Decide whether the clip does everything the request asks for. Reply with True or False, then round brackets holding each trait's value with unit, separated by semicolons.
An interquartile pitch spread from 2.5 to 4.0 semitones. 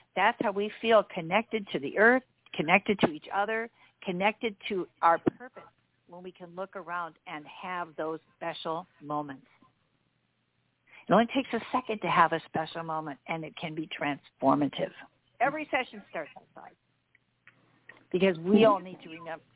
False (4.6 semitones)